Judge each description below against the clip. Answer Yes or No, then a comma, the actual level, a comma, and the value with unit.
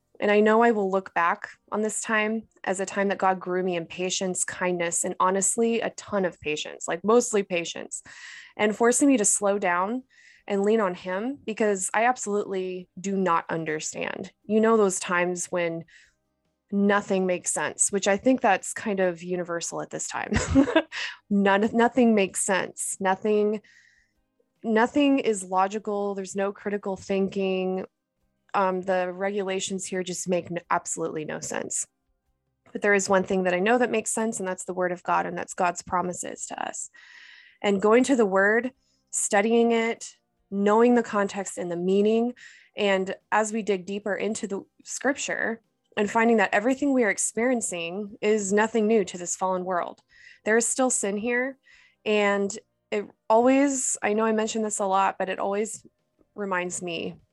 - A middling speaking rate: Yes, average, 170 wpm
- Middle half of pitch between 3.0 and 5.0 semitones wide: Yes, average, 3.4 semitones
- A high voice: Yes, high, 200 Hz